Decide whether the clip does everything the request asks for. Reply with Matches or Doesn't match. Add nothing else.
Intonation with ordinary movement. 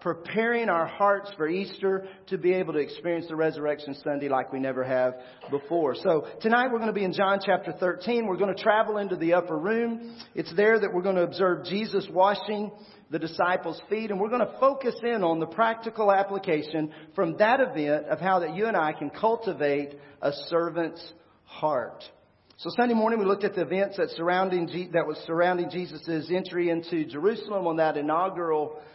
Matches